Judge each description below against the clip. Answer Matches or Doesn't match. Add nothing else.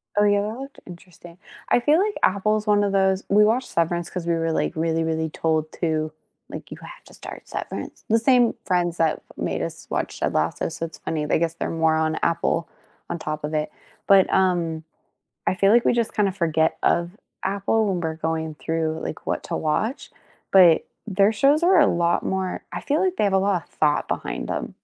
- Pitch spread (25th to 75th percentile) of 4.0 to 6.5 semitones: Matches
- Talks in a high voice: Doesn't match